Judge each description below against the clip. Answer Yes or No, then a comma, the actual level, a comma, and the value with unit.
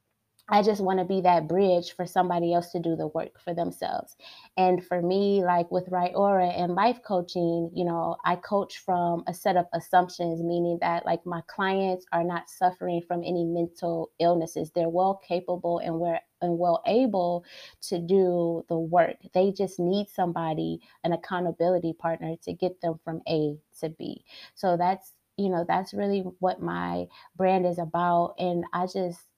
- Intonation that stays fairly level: Yes, narrow, 1.5 semitones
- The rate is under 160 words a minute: No, average, 175 wpm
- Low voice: No, medium, 175 Hz